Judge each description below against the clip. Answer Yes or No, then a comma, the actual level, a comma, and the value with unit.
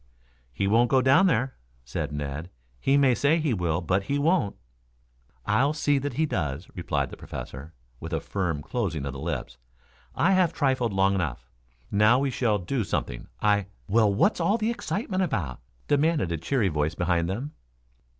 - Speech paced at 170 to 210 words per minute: Yes, average, 180 wpm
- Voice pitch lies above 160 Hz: No, low, 105 Hz